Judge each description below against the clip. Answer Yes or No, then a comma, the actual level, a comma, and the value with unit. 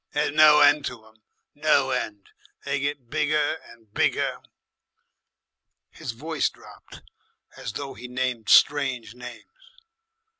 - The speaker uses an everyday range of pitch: Yes, average, 3.7 semitones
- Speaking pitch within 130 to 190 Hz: Yes, low, 135 Hz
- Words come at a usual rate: No, slow, 120 wpm